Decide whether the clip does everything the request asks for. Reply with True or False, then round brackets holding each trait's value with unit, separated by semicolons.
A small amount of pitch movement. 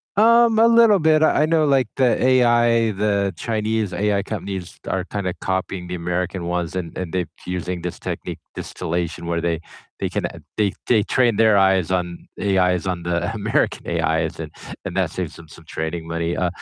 False (4.6 semitones)